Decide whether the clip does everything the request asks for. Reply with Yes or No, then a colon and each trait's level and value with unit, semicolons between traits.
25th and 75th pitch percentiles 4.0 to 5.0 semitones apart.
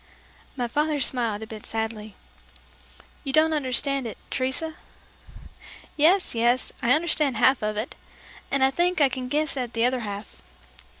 Yes: average, 4.4 semitones